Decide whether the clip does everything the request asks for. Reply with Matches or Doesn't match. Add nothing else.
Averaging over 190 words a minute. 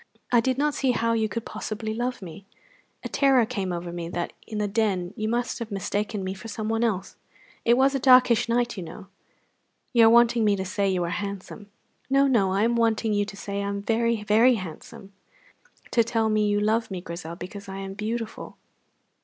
Matches